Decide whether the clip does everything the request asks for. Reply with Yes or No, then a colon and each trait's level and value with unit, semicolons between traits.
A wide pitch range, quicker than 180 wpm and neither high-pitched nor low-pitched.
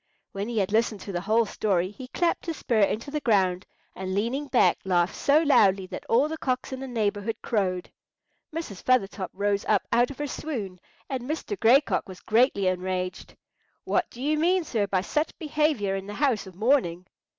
No: wide, 6.3 semitones; average, 195 wpm; high, 220 Hz